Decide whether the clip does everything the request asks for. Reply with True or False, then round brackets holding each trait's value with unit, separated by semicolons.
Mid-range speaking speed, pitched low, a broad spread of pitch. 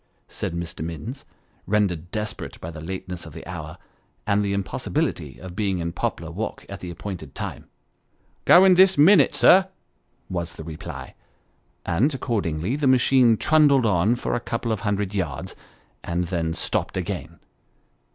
True (160 wpm; 95 Hz; 6.0 semitones)